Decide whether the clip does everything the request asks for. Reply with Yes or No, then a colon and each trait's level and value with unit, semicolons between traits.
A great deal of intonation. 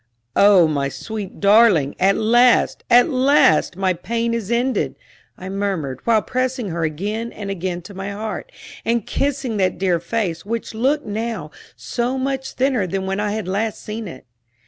No: average, 4.0 semitones